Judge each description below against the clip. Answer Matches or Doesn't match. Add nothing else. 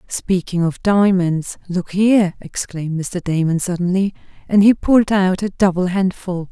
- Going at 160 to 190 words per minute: Doesn't match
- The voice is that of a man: Doesn't match